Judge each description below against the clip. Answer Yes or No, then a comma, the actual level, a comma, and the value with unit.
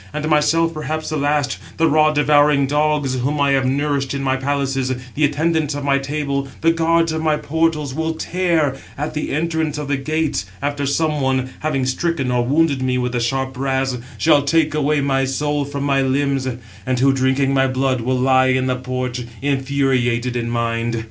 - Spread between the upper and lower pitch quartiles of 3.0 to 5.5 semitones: No, narrow, 2.5 semitones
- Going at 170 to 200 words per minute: Yes, average, 190 wpm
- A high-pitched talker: No, medium, 140 Hz